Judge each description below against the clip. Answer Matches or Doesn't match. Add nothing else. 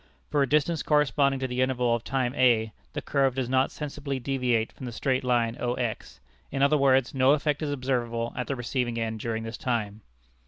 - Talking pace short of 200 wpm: Doesn't match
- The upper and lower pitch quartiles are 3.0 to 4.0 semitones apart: Doesn't match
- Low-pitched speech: Matches